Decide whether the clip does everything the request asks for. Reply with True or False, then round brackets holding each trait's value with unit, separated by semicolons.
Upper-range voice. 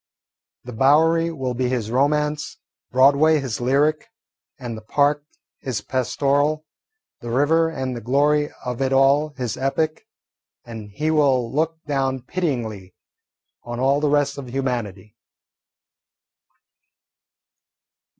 False (135 Hz)